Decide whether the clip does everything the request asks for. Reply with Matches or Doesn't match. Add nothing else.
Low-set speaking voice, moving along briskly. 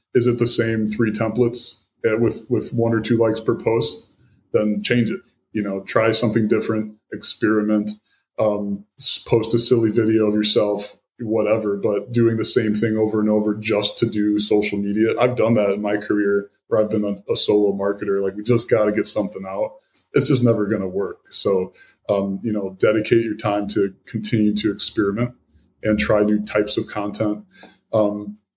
Doesn't match